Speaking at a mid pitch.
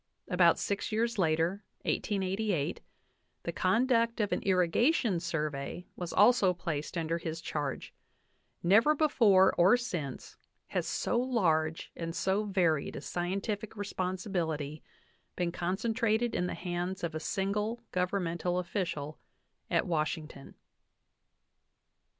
Yes: medium, 180 Hz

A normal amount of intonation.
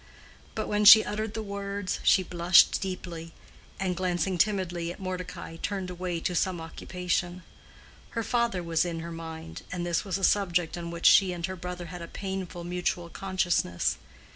No: narrow, 2.0 semitones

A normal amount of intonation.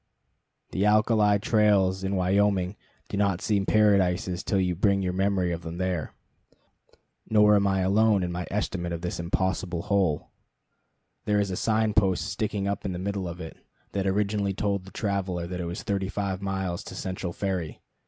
No: narrow, 2.1 semitones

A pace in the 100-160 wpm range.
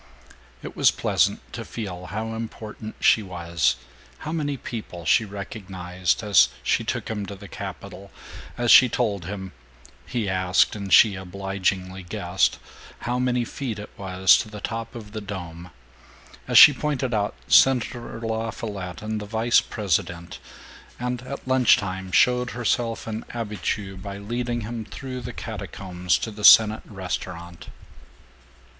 Yes: average, 145 wpm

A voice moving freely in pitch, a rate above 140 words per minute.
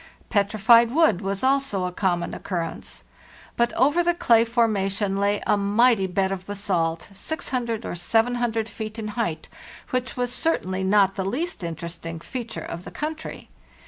No: average, 4.1 semitones; average, 160 wpm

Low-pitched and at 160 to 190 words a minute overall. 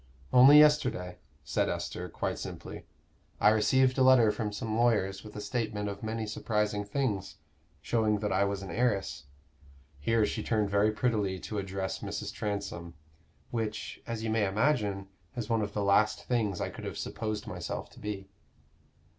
Yes: low, 105 Hz; average, 165 wpm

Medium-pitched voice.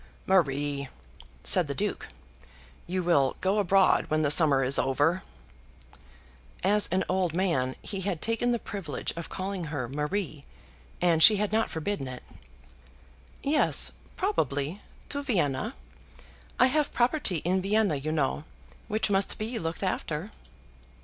Yes: medium, 180 Hz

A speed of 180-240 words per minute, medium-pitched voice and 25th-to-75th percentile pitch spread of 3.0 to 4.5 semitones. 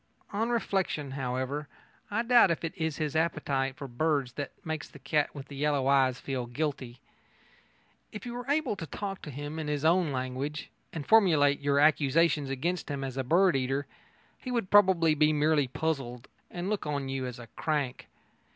Yes: average, 185 wpm; medium, 150 Hz; average, 3.9 semitones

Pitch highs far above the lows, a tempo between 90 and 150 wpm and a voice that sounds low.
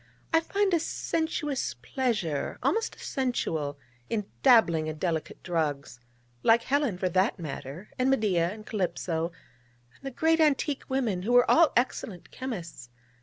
No: wide, 8.3 semitones; average, 145 wpm; high, 215 Hz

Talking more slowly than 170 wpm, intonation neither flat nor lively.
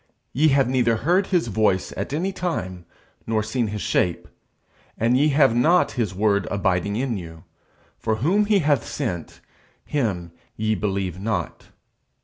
No: average, 150 wpm; wide, 6.4 semitones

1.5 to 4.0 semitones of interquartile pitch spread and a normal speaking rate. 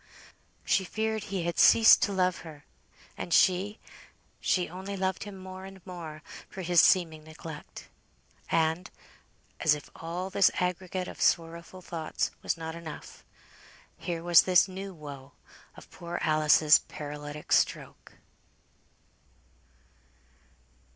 No: average, 2.9 semitones; slow, 125 wpm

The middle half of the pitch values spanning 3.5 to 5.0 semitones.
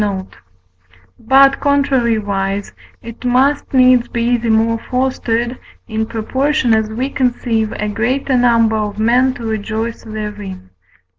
No: average, 2.8 semitones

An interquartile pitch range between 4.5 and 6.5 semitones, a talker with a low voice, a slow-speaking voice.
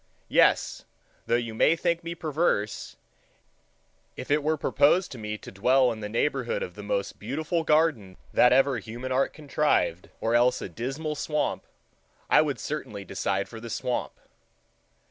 No: wide, 5.5 semitones; low, 130 Hz; average, 165 wpm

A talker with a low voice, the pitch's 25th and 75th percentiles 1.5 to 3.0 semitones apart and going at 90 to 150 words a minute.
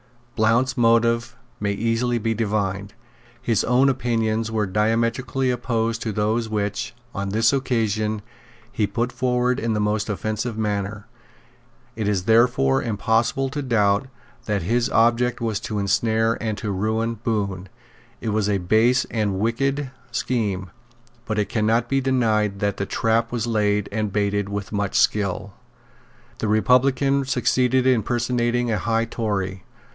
Yes: low, 110 Hz; narrow, 2.5 semitones; average, 145 wpm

